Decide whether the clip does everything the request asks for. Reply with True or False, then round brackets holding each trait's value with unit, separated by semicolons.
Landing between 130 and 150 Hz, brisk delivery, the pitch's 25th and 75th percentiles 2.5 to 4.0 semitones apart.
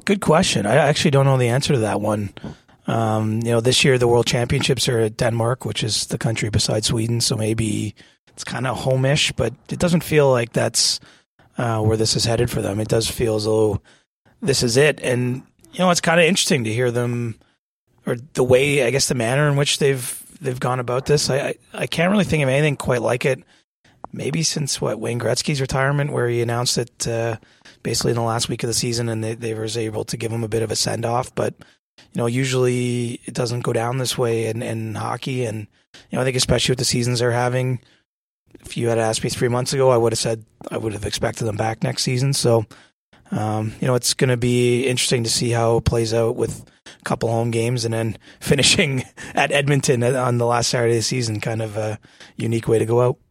False (120 Hz; 230 wpm; 2.8 semitones)